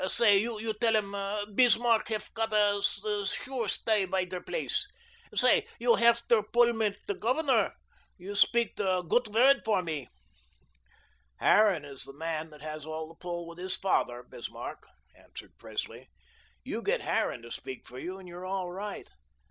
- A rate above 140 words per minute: Yes, average, 160 wpm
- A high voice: Yes, high, 200 Hz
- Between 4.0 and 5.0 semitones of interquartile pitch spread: Yes, average, 4.4 semitones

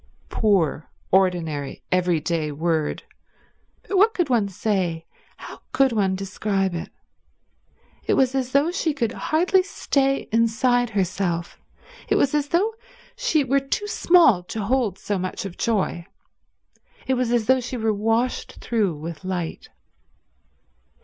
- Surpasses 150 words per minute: No, slow, 135 wpm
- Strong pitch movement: Yes, wide, 6.7 semitones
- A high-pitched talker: Yes, high, 220 Hz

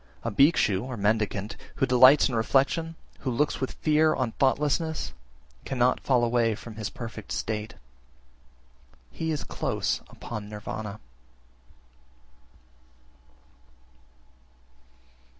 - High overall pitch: No, low, 120 Hz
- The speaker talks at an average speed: No, slow, 100 wpm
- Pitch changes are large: No, average, 4.4 semitones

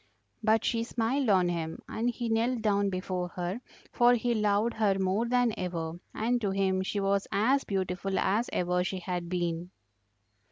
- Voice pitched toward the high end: Yes, high, 200 Hz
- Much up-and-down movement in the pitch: No, average, 4.0 semitones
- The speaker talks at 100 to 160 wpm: No, average, 170 wpm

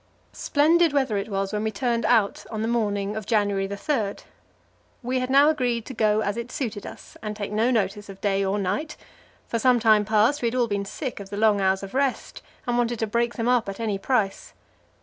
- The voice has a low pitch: No, high, 220 Hz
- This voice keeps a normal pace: No, fast, 225 wpm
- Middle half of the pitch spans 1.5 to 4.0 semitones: Yes, average, 3.4 semitones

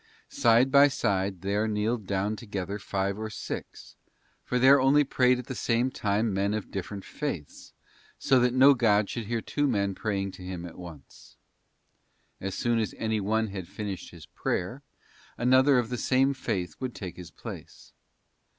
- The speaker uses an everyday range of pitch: Yes, average, 4.3 semitones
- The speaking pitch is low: Yes, low, 110 Hz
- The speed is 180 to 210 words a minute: No, average, 170 wpm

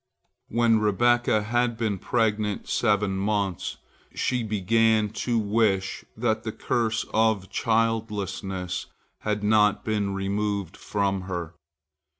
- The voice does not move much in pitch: Yes, narrow, 2.3 semitones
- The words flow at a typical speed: No, slow, 110 wpm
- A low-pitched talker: Yes, low, 105 Hz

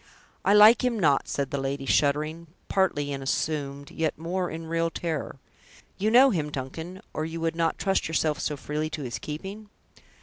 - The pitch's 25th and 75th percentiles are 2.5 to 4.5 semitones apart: Yes, average, 3.9 semitones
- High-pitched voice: No, medium, 160 Hz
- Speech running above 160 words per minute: Yes, average, 180 wpm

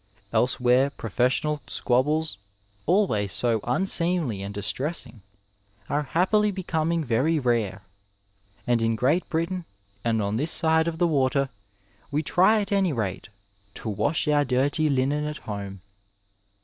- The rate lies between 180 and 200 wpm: No, slow, 135 wpm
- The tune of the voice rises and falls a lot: Yes, wide, 6.0 semitones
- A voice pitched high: No, medium, 140 Hz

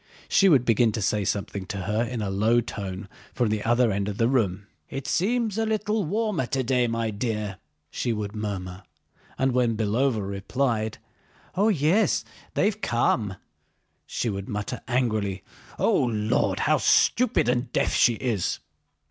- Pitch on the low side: Yes, low, 115 Hz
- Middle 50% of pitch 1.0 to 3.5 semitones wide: No, average, 4.3 semitones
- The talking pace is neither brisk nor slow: Yes, average, 155 wpm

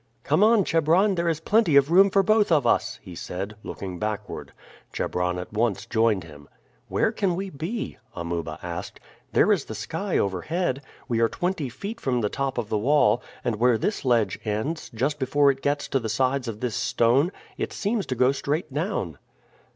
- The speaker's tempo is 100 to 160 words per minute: No, average, 190 wpm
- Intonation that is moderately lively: No, wide, 7.8 semitones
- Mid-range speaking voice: No, low, 130 Hz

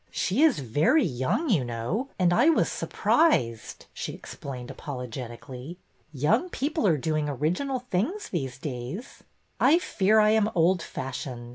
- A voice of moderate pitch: Yes, medium, 165 Hz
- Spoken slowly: No, average, 145 wpm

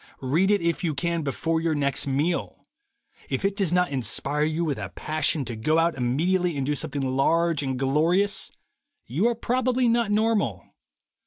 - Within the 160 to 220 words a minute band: Yes, average, 175 wpm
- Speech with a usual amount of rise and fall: Yes, average, 5.0 semitones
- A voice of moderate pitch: Yes, medium, 160 Hz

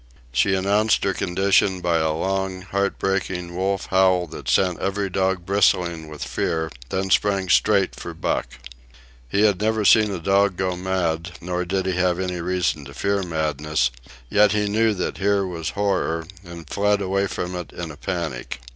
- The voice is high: No, very low, 95 Hz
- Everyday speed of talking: Yes, average, 175 wpm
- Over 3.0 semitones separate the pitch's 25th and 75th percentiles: No, narrow, 2.4 semitones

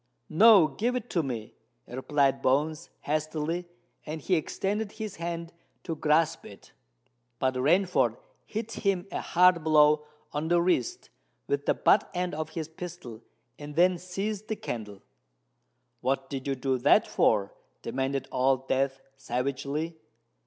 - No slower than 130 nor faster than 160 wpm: Yes, average, 140 wpm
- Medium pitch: Yes, medium, 155 Hz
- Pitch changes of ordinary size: Yes, average, 4.8 semitones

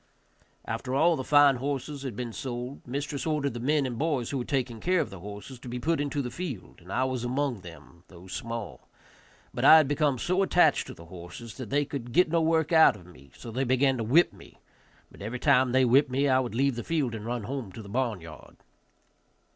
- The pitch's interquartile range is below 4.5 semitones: Yes, average, 3.7 semitones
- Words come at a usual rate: No, fast, 235 wpm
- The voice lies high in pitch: No, low, 130 Hz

